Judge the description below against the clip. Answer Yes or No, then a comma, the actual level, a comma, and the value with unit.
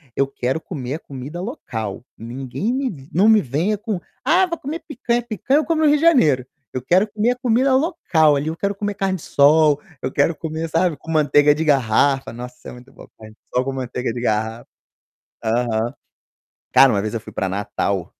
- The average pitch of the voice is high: No, medium, 150 Hz